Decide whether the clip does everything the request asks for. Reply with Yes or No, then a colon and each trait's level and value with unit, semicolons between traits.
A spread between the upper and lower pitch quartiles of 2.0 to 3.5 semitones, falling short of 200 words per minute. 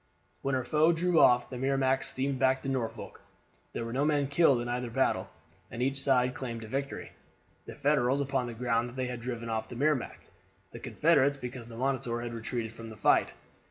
No: narrow, 2.5 semitones; fast, 205 wpm